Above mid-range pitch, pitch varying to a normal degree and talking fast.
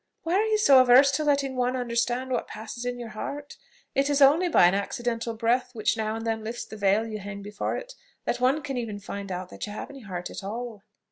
Yes: high, 240 Hz; average, 4.0 semitones; fast, 240 wpm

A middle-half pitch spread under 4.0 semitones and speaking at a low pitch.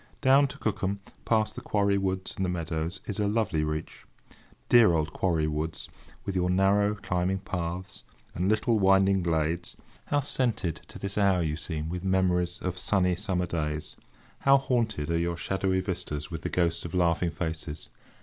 Yes: average, 3.1 semitones; very low, 90 Hz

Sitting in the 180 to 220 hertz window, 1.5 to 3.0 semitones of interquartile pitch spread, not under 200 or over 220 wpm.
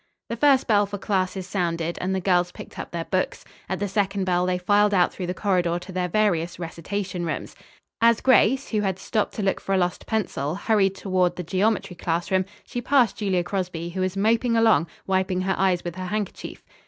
Yes: high, 190 Hz; narrow, 2.6 semitones; fast, 205 wpm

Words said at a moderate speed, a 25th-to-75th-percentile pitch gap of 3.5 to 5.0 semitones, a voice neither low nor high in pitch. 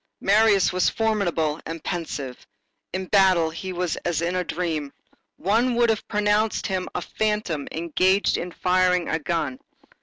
Yes: average, 150 wpm; average, 3.9 semitones; medium, 180 Hz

